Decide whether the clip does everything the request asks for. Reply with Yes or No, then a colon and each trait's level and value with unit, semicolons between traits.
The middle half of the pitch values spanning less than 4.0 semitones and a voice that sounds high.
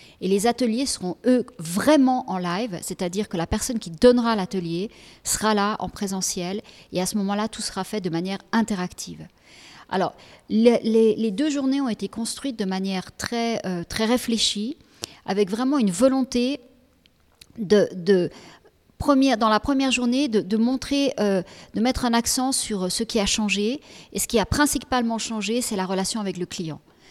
No: average, 4.3 semitones; high, 220 Hz